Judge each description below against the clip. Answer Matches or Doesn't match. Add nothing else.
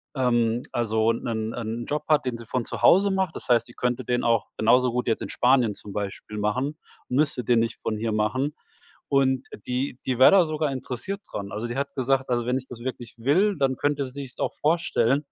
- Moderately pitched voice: Doesn't match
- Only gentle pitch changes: Doesn't match